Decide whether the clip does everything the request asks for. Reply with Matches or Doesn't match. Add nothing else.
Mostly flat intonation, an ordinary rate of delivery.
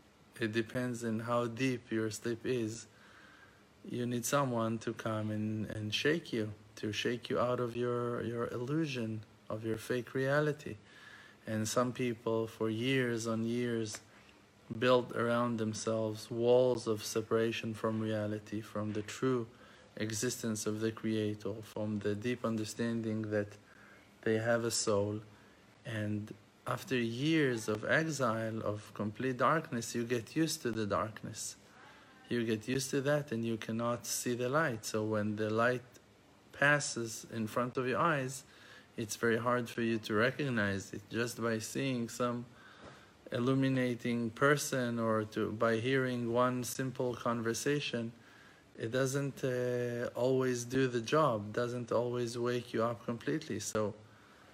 Matches